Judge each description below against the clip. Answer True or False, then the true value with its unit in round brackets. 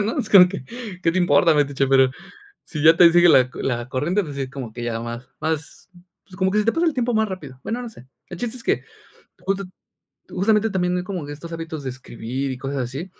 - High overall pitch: False (165 Hz)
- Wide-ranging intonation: True (6.2 semitones)